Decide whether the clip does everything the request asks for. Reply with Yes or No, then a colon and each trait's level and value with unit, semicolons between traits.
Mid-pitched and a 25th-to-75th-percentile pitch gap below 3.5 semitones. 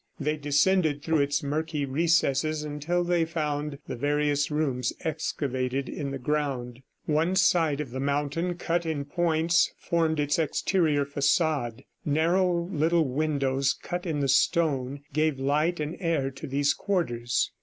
Yes: medium, 150 Hz; average, 2.7 semitones